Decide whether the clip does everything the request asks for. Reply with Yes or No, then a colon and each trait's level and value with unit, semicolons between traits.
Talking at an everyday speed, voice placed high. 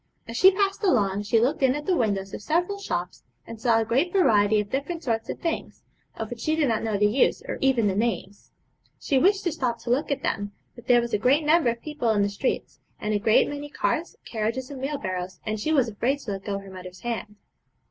No: fast, 240 wpm; high, 235 Hz